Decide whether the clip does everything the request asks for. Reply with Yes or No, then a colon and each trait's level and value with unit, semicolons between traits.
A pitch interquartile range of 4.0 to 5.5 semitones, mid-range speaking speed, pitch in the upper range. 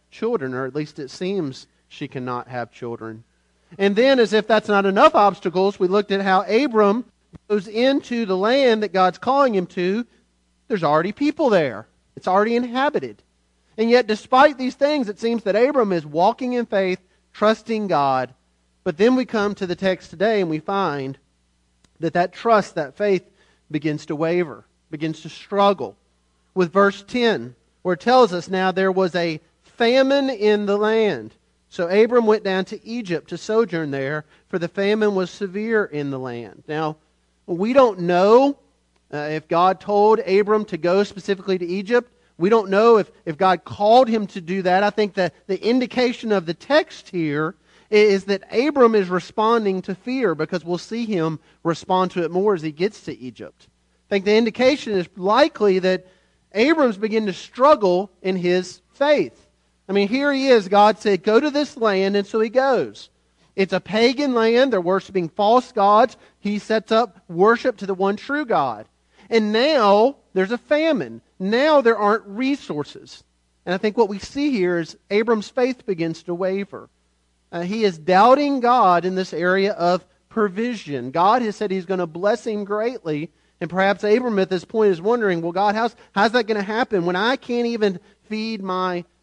Yes: average, 4.4 semitones; average, 180 wpm; high, 200 Hz